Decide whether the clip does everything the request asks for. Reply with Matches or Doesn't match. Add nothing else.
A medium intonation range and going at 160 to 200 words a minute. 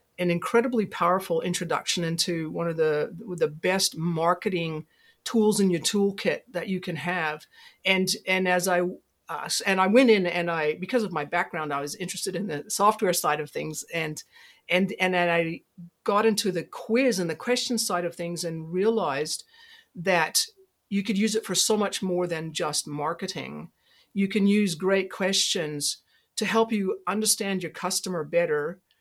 Matches